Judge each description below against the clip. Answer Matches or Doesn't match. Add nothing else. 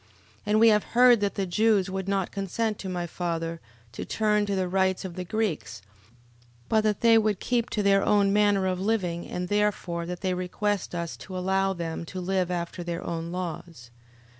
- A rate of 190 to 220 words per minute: Matches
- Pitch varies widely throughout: Doesn't match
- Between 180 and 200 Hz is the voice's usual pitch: Matches